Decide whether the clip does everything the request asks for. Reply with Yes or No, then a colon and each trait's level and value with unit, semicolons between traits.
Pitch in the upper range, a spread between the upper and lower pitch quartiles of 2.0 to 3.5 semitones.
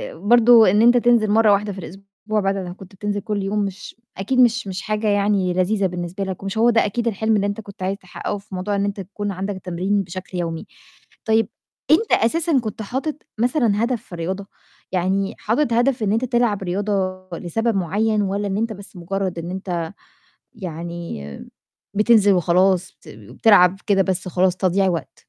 Yes: high, 200 Hz; average, 2.8 semitones